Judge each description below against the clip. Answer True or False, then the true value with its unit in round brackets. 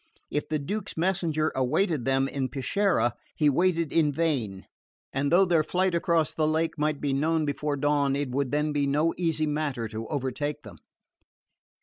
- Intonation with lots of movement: False (3.0 semitones)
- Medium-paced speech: True (170 wpm)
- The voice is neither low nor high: True (150 Hz)